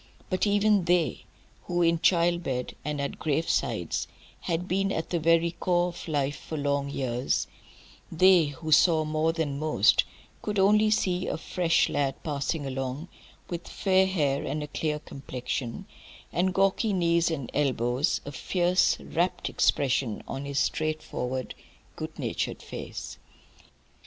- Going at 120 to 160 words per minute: Yes, average, 140 wpm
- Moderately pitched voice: Yes, medium, 160 Hz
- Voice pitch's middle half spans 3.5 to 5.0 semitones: Yes, average, 4.0 semitones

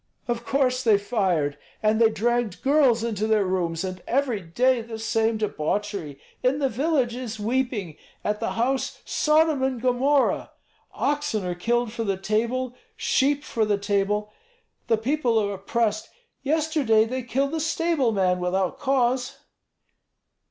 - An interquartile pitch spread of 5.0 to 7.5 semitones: No, average, 4.1 semitones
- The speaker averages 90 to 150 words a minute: Yes, average, 145 wpm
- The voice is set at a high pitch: Yes, high, 230 Hz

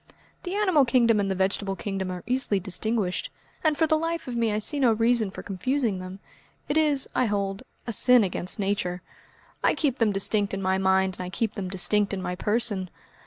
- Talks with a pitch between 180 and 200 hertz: No, high, 210 Hz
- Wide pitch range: No, average, 4.5 semitones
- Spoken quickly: Yes, fast, 210 wpm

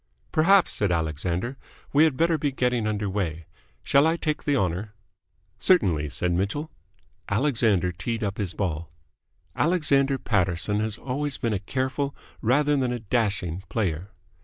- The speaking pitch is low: Yes, low, 110 Hz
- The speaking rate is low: No, average, 145 wpm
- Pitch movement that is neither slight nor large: No, wide, 7.3 semitones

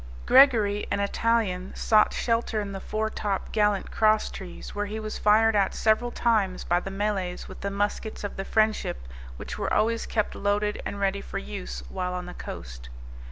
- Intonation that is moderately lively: No, narrow, 2.2 semitones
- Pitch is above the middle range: Yes, high, 205 Hz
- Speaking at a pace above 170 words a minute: Yes, average, 180 wpm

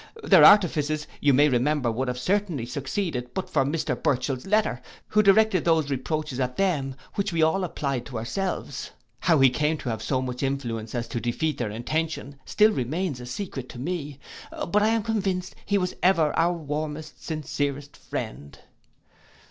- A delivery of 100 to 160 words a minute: No, average, 170 wpm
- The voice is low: No, medium, 150 Hz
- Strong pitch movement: Yes, wide, 5.8 semitones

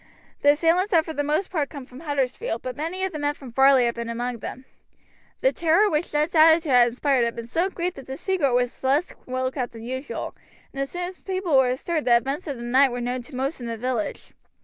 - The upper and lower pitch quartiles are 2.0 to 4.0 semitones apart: No, average, 4.5 semitones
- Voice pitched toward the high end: Yes, very high, 275 Hz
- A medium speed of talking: No, fast, 250 wpm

